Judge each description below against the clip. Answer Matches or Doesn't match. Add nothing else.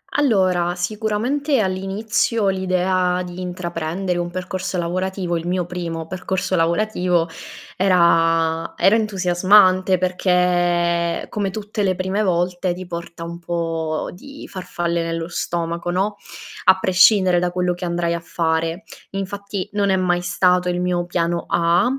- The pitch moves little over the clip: Matches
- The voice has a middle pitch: Matches